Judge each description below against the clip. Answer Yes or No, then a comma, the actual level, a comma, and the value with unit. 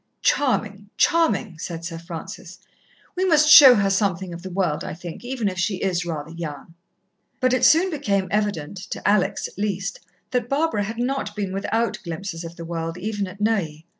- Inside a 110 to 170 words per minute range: No, average, 185 wpm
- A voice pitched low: No, high, 195 Hz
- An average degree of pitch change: Yes, average, 4.9 semitones